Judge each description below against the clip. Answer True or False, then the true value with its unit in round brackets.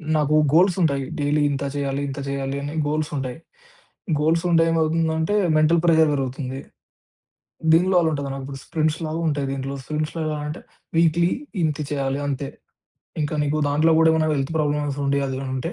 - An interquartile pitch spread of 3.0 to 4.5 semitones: False (2.6 semitones)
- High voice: False (150 Hz)